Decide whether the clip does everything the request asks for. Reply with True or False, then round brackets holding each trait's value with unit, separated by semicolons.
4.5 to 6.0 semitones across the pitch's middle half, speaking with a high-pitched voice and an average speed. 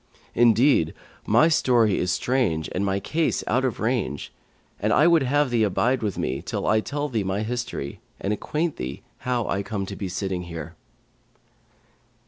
False (5.2 semitones; 110 Hz; 170 wpm)